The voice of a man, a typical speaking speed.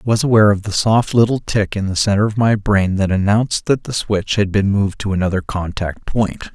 No: male; fast, 240 wpm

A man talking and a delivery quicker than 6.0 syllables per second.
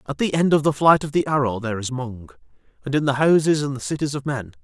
Yes: male; 6.5 syllables/s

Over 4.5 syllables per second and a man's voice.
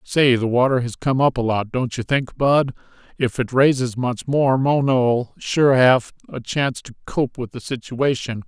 No: 4.3 syllables/s; male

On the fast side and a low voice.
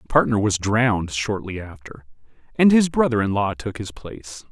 No: average, 185 wpm; low, 110 Hz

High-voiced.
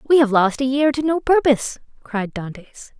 Yes: very high, 255 Hz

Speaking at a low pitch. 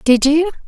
No: very high, 305 Hz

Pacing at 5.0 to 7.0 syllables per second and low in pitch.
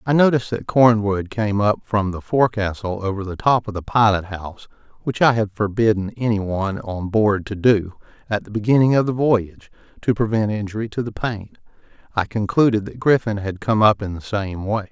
Yes: 5.4 syllables/s; low, 105 Hz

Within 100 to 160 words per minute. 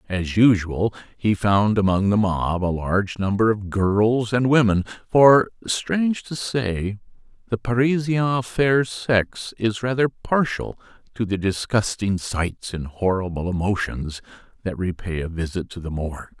Yes: average, 145 wpm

